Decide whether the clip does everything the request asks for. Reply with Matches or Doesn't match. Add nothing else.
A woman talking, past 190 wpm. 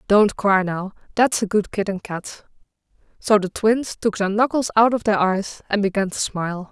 Matches